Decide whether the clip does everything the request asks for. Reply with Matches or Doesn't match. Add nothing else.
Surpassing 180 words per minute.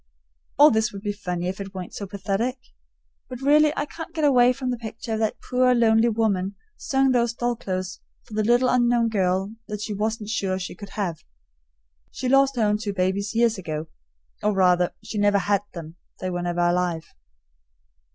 Matches